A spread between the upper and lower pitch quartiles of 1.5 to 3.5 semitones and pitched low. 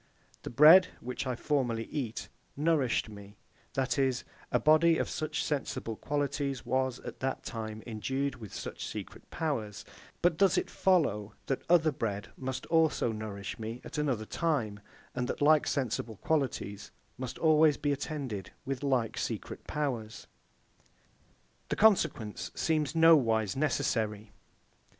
No: average, 5.3 semitones; low, 130 Hz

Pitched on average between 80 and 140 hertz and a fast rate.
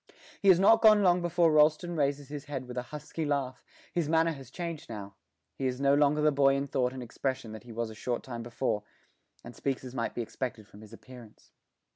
Yes: low, 135 Hz; fast, 225 wpm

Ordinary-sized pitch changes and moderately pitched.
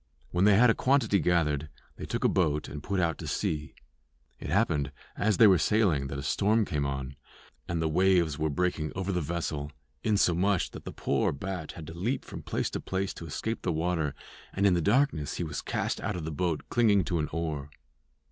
No: average, 4.4 semitones; very low, 85 Hz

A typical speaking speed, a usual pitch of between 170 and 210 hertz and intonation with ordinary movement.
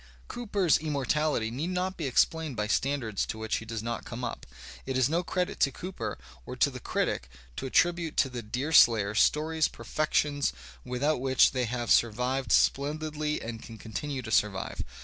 No: average, 175 wpm; low, 135 Hz; average, 5.0 semitones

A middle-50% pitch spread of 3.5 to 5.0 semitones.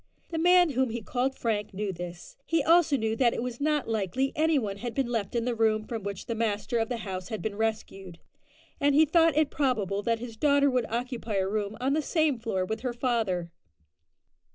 Yes: average, 4.6 semitones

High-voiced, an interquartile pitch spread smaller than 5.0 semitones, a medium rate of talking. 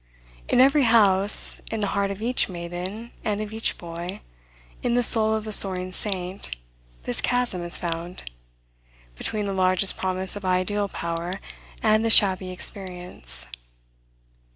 Yes: high, 195 Hz; average, 3.1 semitones; average, 145 wpm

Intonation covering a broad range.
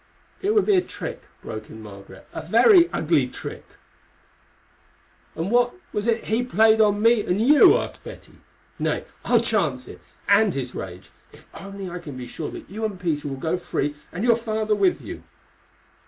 Yes: wide, 7.6 semitones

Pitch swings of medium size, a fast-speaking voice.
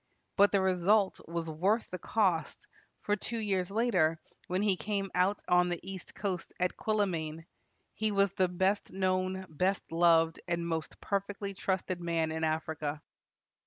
No: average, 3.0 semitones; average, 155 wpm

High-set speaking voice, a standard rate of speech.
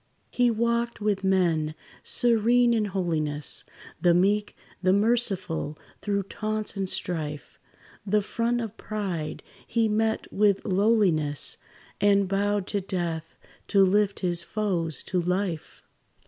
No: high, 200 Hz; slow, 120 wpm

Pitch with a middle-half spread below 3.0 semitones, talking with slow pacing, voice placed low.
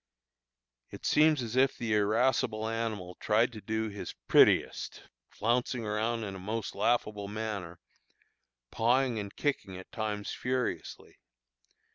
Yes: narrow, 2.4 semitones; slow, 125 wpm; low, 110 Hz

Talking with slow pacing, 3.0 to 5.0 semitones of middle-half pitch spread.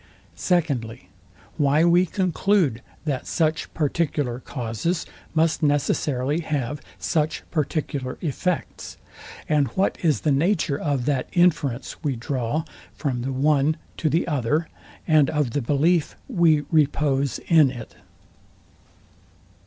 Yes: slow, 115 wpm; average, 3.3 semitones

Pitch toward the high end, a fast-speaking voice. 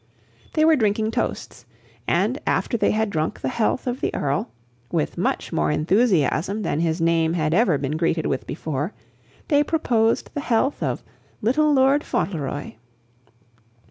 No: high, 195 Hz; average, 150 wpm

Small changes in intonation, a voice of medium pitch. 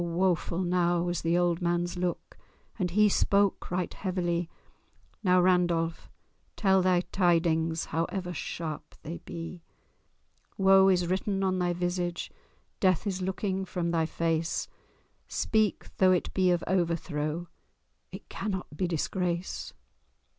Yes: narrow, 1.7 semitones; medium, 175 Hz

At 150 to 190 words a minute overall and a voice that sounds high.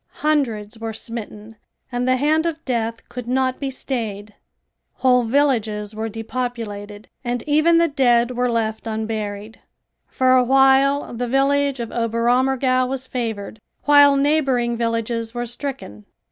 No: slow, 135 wpm; high, 245 Hz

